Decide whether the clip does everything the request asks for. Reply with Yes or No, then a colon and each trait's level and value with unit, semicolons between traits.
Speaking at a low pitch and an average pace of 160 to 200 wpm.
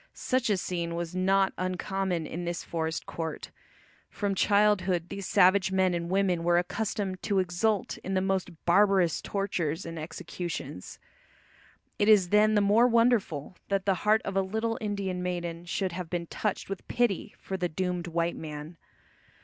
No: medium, 185 Hz; average, 165 wpm